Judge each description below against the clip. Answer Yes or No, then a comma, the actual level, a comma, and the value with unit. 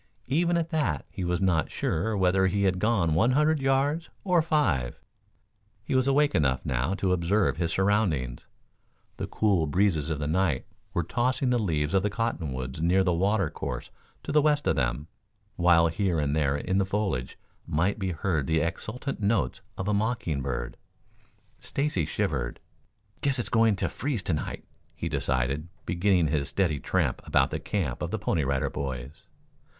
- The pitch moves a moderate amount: No, wide, 6.5 semitones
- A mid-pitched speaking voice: No, very low, 95 Hz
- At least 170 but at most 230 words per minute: Yes, average, 175 wpm